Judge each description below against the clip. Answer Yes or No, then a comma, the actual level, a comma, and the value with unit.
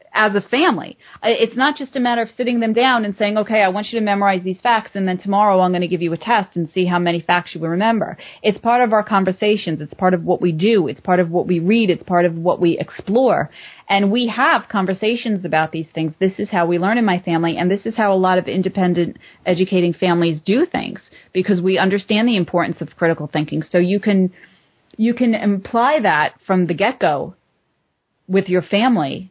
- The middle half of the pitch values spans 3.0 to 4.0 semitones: Yes, average, 3.5 semitones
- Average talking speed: No, fast, 225 wpm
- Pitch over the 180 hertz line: Yes, high, 190 Hz